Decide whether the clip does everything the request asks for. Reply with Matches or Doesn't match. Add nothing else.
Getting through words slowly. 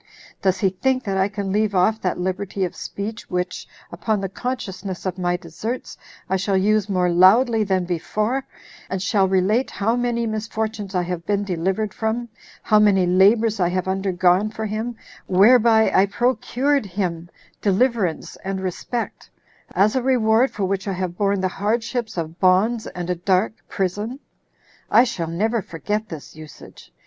Doesn't match